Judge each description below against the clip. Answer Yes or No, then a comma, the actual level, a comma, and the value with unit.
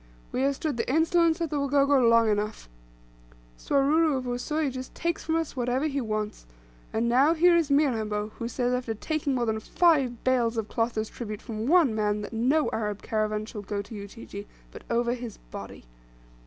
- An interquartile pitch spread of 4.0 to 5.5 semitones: Yes, average, 4.7 semitones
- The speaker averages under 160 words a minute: No, average, 190 wpm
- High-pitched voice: Yes, high, 245 Hz